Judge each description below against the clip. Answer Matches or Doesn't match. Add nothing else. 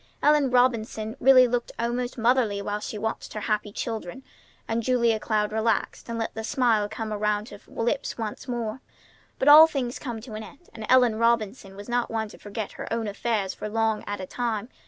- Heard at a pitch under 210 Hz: Doesn't match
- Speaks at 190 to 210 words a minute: Matches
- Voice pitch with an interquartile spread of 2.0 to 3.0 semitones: Matches